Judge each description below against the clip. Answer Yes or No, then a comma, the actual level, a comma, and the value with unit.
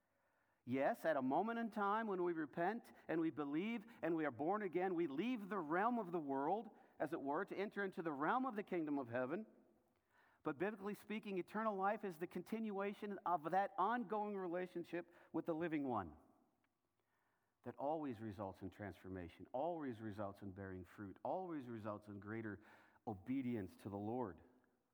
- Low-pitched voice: No, medium, 170 Hz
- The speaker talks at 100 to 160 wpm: No, average, 170 wpm